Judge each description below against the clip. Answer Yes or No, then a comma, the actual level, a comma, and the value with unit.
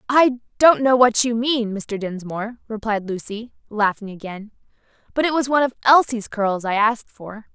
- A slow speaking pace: No, average, 175 wpm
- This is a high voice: Yes, high, 225 Hz